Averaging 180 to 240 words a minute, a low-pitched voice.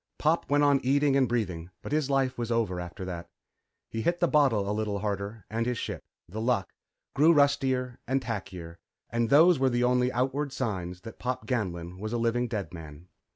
Yes: average, 200 wpm; low, 120 Hz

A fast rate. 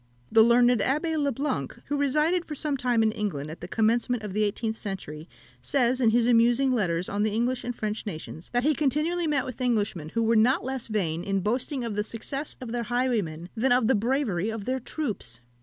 Yes: fast, 215 wpm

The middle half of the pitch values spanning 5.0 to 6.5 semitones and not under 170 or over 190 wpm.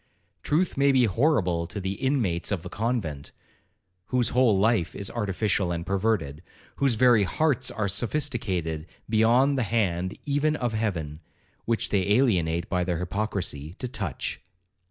No: wide, 5.6 semitones; average, 140 wpm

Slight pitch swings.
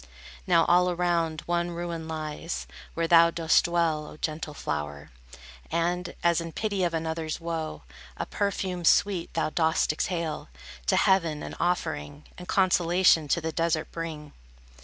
Yes: narrow, 1.7 semitones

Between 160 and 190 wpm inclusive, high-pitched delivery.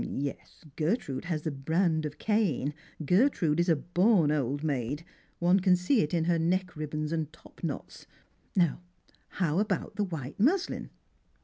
No: average, 165 wpm; medium, 165 Hz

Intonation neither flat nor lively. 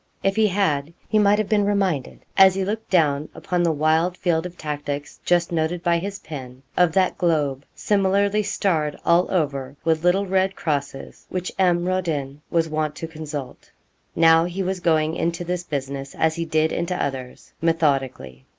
Yes: average, 3.8 semitones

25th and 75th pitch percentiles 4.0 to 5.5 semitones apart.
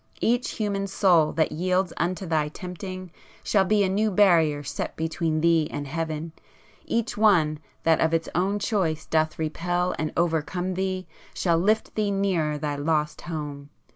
No: average, 3.5 semitones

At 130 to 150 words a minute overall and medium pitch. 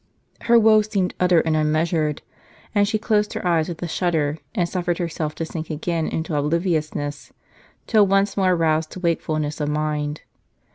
No: average, 165 wpm; medium, 165 Hz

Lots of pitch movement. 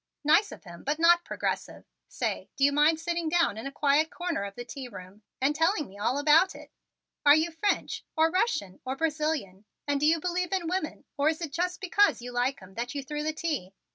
No: average, 4.6 semitones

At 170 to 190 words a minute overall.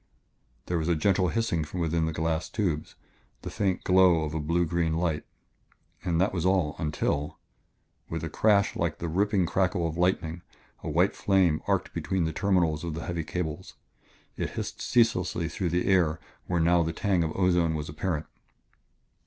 Yes: average, 175 wpm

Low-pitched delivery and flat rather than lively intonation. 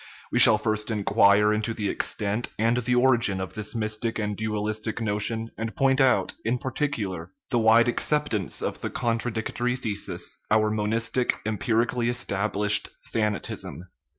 Yes: low, 110 Hz; narrow, 2.1 semitones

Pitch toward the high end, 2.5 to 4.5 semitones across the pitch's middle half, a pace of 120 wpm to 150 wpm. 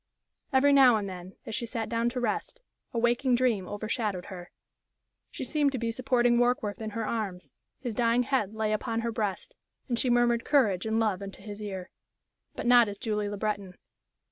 No: high, 225 Hz; average, 2.9 semitones; average, 195 wpm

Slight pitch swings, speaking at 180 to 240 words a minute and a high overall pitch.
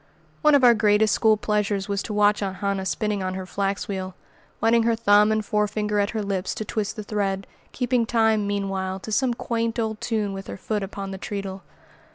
Yes: narrow, 2.0 semitones; fast, 205 wpm; high, 210 Hz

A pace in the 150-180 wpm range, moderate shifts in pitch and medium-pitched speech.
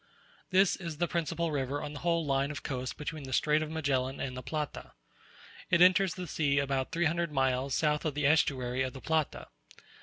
No: fast, 205 wpm; average, 3.4 semitones; medium, 150 Hz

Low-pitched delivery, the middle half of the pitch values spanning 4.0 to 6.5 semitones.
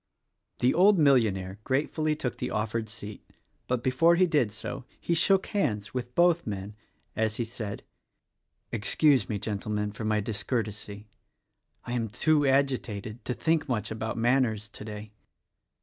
Yes: low, 115 Hz; average, 4.7 semitones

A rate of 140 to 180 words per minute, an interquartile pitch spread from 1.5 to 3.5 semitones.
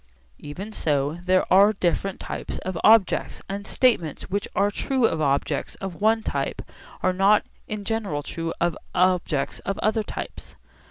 No: average, 155 wpm; average, 4.0 semitones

